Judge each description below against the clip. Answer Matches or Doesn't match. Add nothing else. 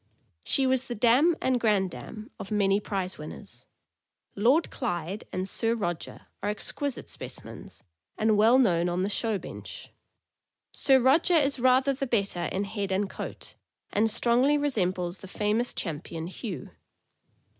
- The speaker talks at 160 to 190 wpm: Doesn't match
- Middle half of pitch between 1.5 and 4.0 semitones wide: Doesn't match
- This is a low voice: Doesn't match